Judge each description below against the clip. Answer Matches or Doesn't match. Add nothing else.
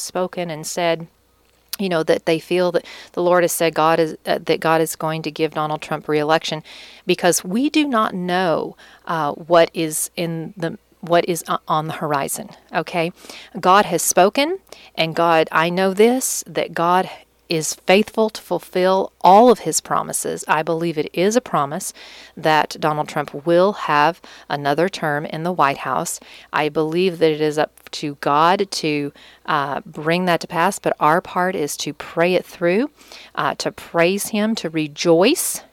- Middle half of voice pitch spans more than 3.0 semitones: Doesn't match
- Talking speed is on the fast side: Doesn't match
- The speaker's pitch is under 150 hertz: Doesn't match